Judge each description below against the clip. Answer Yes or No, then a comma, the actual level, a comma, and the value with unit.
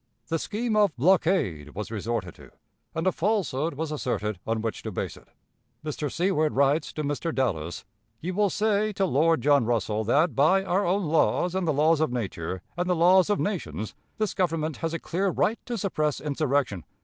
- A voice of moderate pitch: Yes, medium, 155 Hz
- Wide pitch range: Yes, wide, 6.7 semitones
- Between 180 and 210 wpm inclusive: Yes, average, 190 wpm